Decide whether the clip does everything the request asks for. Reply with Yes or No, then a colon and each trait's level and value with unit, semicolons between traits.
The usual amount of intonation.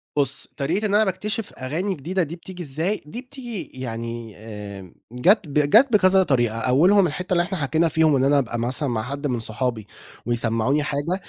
No: wide, 7.4 semitones